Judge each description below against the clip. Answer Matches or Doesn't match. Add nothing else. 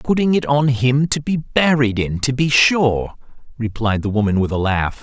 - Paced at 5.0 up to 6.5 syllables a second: Doesn't match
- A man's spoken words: Matches